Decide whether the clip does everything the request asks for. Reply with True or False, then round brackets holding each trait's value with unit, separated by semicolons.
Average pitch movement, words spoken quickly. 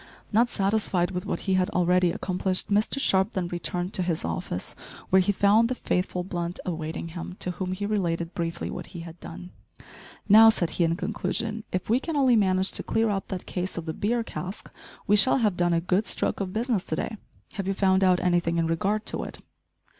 True (3.0 semitones; 215 wpm)